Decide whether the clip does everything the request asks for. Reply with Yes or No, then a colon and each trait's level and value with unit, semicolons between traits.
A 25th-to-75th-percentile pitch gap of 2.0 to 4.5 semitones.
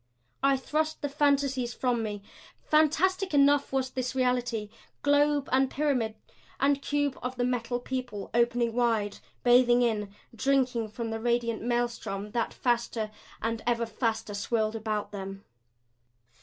Yes: average, 3.3 semitones